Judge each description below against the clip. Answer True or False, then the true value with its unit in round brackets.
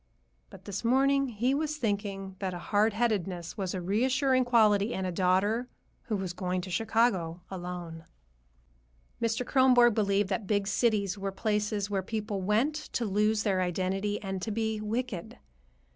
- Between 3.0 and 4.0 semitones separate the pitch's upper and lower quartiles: True (3.3 semitones)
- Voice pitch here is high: True (205 Hz)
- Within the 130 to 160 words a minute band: True (155 wpm)